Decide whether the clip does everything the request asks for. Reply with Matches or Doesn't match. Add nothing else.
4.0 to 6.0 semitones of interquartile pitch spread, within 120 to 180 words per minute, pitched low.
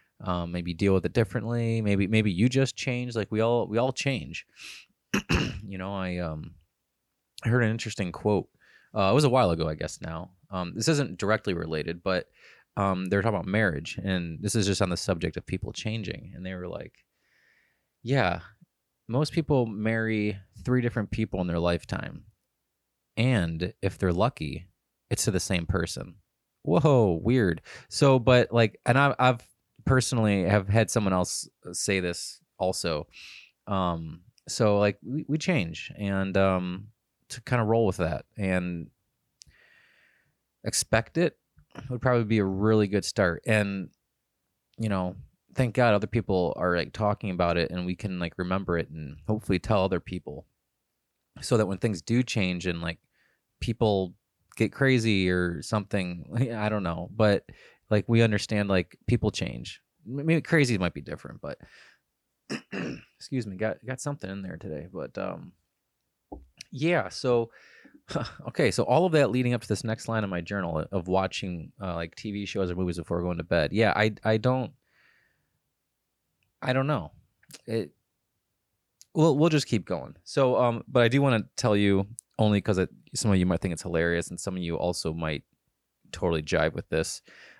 Matches